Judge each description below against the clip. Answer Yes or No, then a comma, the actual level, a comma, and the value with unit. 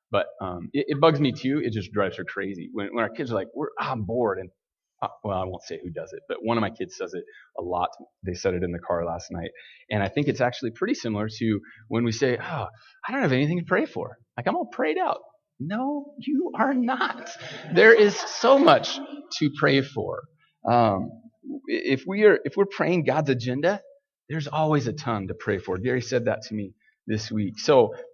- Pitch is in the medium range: Yes, medium, 160 Hz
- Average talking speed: No, fast, 230 wpm